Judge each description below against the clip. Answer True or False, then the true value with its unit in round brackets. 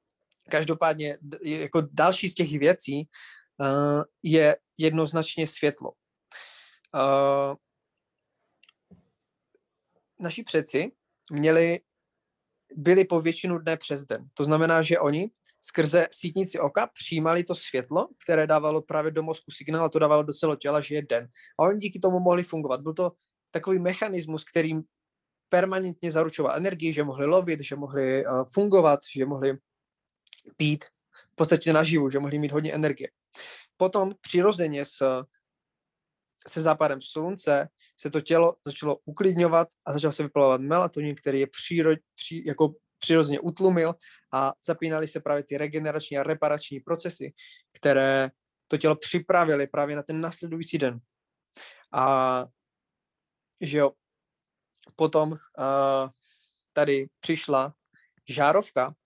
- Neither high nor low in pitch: True (155 Hz)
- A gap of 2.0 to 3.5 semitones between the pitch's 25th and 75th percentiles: True (2.9 semitones)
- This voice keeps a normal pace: True (125 wpm)